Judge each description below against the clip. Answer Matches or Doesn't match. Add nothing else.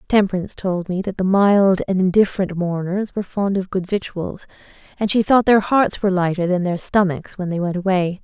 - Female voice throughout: Matches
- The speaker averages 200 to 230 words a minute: Matches